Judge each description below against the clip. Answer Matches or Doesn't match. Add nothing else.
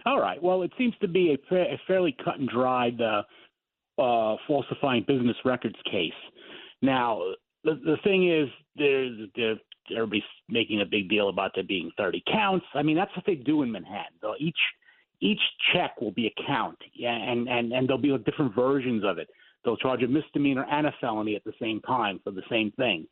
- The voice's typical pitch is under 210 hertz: Matches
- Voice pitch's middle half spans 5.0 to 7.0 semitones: Matches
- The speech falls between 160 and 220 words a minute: Matches